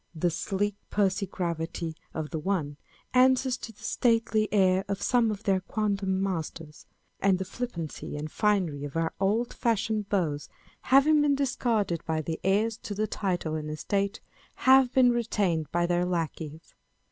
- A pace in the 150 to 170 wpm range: Yes, average, 160 wpm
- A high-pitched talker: Yes, high, 195 Hz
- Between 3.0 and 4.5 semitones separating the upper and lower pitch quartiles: No, average, 5.1 semitones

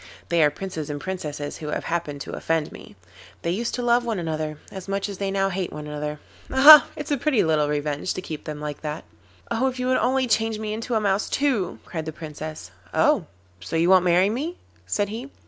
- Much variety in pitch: Yes, wide, 6.7 semitones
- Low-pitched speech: No, medium, 185 Hz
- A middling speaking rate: No, fast, 225 wpm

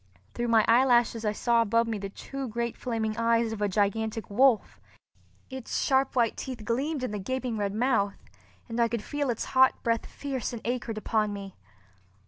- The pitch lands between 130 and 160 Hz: No, high, 230 Hz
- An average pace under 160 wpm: No, average, 185 wpm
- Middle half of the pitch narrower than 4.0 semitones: Yes, average, 2.8 semitones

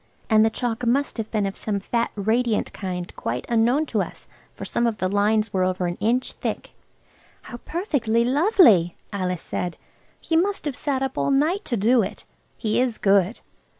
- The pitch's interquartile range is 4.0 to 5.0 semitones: Yes, average, 4.5 semitones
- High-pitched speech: Yes, high, 225 Hz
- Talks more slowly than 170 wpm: No, average, 185 wpm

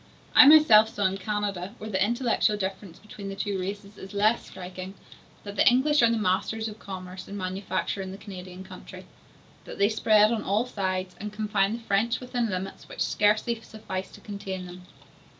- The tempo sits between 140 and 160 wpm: No, average, 185 wpm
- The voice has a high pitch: Yes, high, 205 Hz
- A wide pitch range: No, narrow, 2.5 semitones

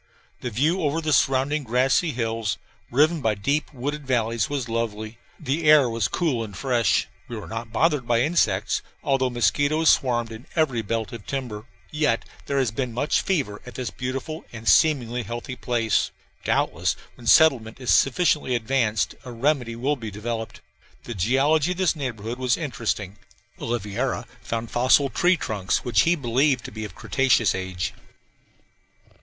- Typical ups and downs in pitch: Yes, average, 4.0 semitones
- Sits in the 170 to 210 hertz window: No, low, 125 Hz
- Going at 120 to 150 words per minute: No, average, 160 wpm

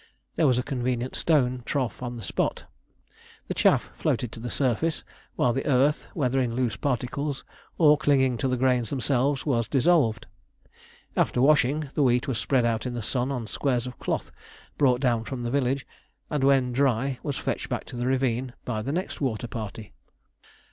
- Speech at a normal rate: Yes, average, 180 wpm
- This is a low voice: Yes, low, 130 Hz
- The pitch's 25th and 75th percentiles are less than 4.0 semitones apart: Yes, narrow, 2.4 semitones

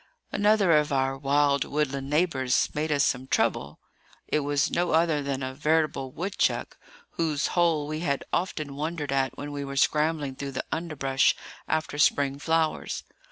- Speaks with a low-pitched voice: No, medium, 145 Hz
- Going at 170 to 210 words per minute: No, average, 160 wpm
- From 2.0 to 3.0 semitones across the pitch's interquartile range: Yes, narrow, 2.5 semitones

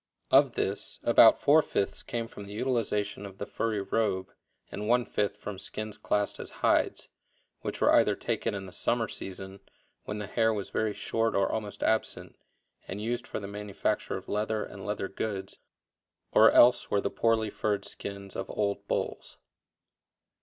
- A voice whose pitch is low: Yes, low, 105 Hz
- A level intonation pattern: Yes, narrow, 2.1 semitones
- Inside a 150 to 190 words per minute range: Yes, average, 170 wpm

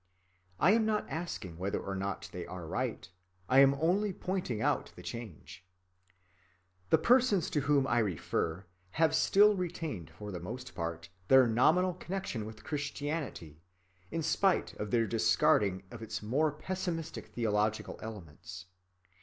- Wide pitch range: Yes, wide, 8.9 semitones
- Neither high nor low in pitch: No, low, 120 Hz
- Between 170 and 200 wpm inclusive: No, average, 145 wpm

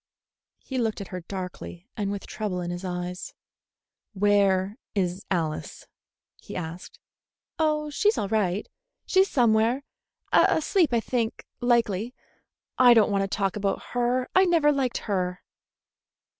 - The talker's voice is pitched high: Yes, high, 210 Hz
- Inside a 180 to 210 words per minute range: No, slow, 135 wpm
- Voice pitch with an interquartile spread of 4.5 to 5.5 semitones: Yes, average, 5.0 semitones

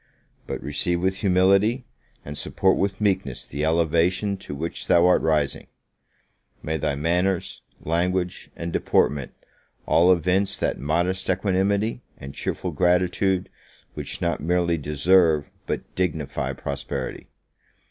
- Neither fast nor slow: No, slow, 120 wpm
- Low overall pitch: Yes, very low, 85 Hz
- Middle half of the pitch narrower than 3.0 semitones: No, average, 3.6 semitones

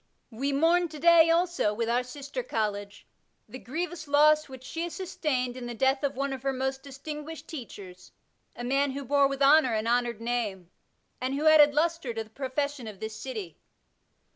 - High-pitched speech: Yes, very high, 270 Hz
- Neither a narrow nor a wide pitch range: Yes, average, 4.2 semitones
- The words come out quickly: No, average, 190 wpm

